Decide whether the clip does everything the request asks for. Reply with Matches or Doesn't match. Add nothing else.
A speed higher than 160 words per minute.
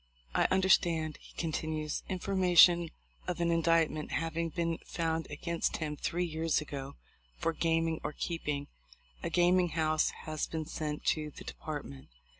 Doesn't match